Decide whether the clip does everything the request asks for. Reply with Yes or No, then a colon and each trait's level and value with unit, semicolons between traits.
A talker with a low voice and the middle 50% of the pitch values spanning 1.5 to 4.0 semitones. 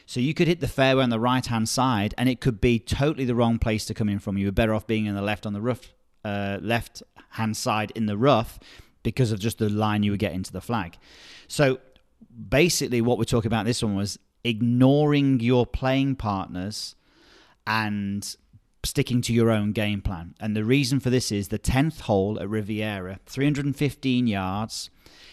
Yes: low, 115 Hz; average, 3.5 semitones